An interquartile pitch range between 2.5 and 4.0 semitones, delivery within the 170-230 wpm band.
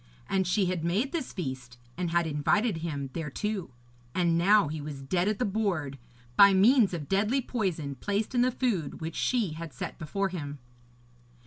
No: average, 5.3 semitones; average, 180 wpm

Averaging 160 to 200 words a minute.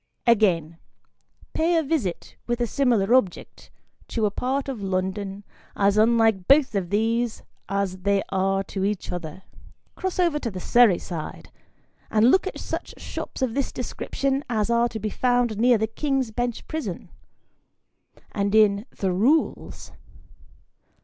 No: average, 150 wpm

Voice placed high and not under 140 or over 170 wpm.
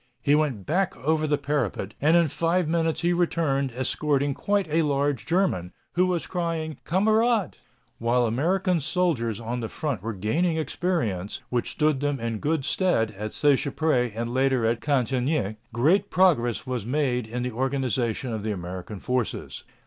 No: medium, 140 Hz; average, 160 wpm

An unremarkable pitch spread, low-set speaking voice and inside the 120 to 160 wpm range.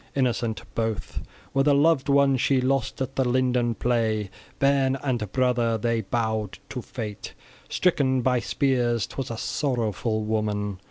Yes: average, 3.3 semitones; low, 120 Hz; average, 150 wpm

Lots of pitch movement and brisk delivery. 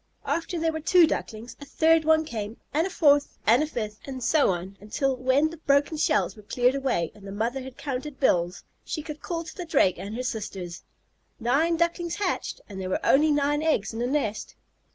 Yes: wide, 6.3 semitones; fast, 215 wpm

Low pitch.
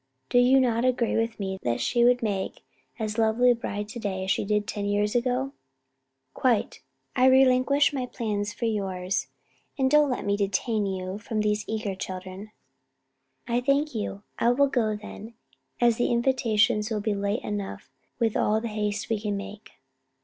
No: high, 220 Hz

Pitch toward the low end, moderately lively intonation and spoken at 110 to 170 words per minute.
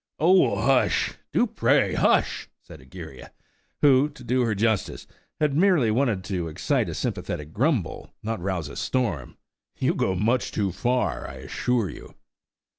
No: low, 115 Hz; wide, 5.8 semitones; average, 150 wpm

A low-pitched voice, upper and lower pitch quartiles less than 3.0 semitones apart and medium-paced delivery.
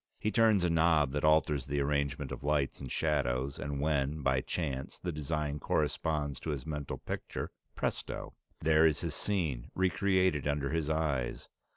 Yes: very low, 75 Hz; narrow, 2.5 semitones; average, 170 wpm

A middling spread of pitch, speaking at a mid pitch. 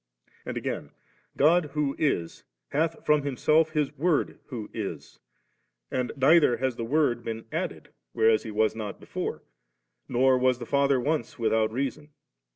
No: average, 4.8 semitones; low, 130 Hz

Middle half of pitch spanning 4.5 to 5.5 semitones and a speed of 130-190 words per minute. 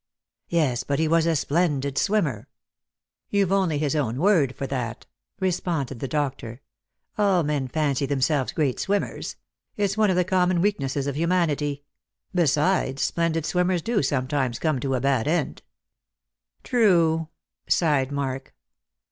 Yes: average, 4.8 semitones; average, 150 wpm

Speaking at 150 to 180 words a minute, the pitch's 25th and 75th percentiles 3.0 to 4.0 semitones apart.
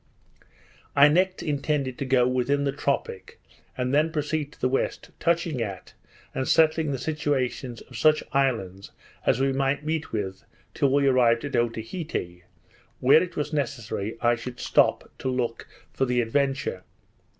Yes: average, 155 wpm; average, 3.7 semitones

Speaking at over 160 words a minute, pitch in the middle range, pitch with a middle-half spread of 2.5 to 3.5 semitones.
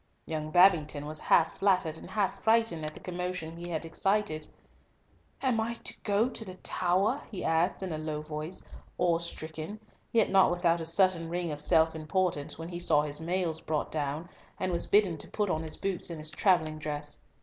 Yes: average, 190 wpm; medium, 170 Hz; average, 3.2 semitones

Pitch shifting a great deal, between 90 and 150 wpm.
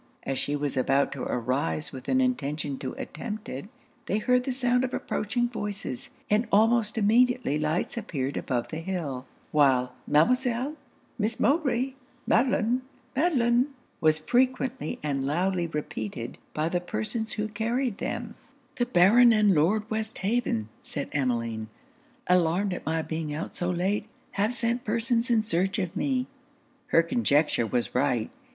Yes: wide, 8.4 semitones; average, 145 wpm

